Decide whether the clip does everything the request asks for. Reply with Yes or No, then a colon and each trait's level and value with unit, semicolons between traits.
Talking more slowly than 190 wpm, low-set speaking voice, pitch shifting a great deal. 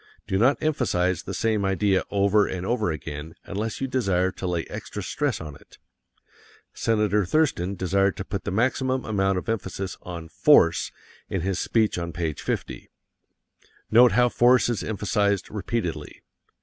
No: average, 155 wpm; low, 100 Hz; average, 4.1 semitones